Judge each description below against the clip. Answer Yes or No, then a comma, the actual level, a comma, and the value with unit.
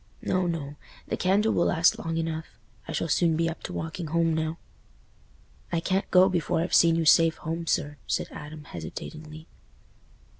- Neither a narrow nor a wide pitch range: No, narrow, 1.4 semitones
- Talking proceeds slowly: No, average, 165 wpm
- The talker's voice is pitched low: No, medium, 165 Hz